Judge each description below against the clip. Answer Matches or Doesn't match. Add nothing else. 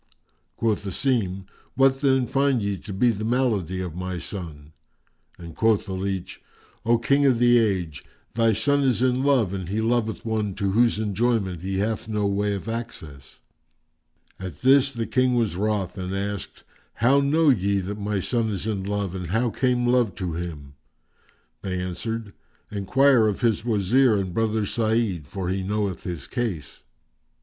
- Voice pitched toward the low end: Matches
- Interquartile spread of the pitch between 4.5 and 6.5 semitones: Doesn't match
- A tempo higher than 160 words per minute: Matches